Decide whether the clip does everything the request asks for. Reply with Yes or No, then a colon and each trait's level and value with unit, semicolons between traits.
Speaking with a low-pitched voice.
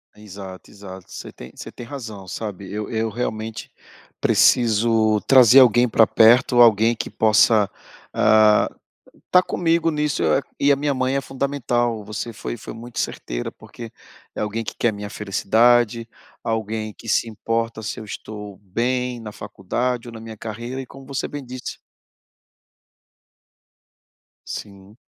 Yes: low, 115 Hz